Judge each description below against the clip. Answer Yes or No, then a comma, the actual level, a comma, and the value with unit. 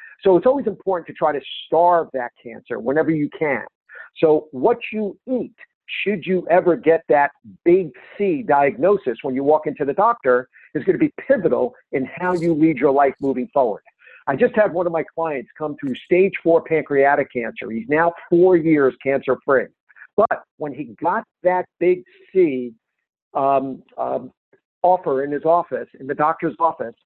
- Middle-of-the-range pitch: Yes, medium, 165 Hz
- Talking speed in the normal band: Yes, average, 175 wpm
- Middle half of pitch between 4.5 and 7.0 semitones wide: Yes, average, 5.1 semitones